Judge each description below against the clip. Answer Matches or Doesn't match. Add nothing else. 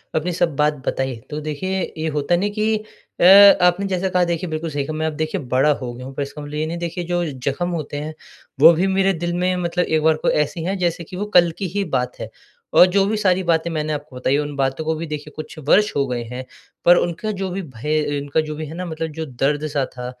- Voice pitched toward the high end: Doesn't match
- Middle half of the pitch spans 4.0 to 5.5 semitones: Doesn't match